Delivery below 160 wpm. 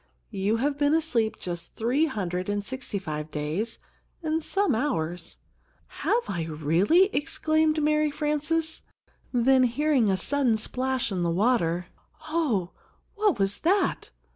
Yes: slow, 135 wpm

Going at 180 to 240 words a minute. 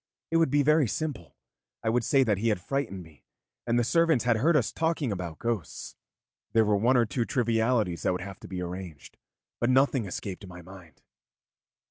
Yes: average, 195 wpm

